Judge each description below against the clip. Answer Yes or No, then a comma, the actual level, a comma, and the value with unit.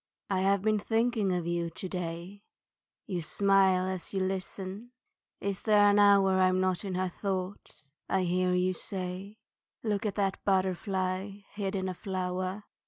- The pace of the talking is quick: No, average, 160 wpm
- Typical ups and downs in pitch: No, narrow, 1.6 semitones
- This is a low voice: No, high, 190 Hz